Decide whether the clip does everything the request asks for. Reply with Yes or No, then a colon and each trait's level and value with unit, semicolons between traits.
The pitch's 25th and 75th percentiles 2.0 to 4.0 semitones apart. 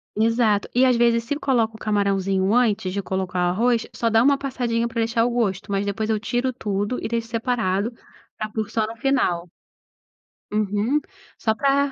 Yes: average, 2.9 semitones